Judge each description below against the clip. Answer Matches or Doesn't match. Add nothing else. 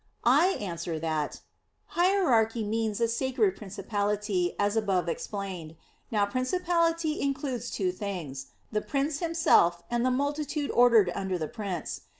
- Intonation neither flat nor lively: Doesn't match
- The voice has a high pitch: Matches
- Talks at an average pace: Doesn't match